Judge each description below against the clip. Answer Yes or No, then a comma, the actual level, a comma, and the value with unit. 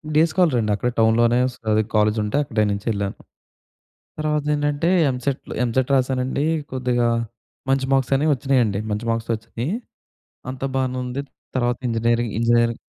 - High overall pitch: No, low, 120 Hz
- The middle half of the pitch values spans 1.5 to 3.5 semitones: Yes, average, 2.8 semitones